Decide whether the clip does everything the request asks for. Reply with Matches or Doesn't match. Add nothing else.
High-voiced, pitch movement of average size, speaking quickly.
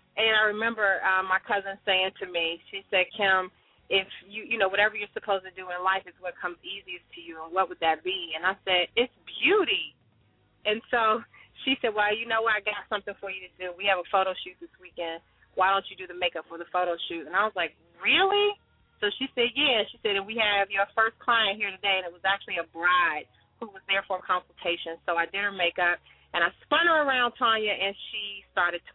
Matches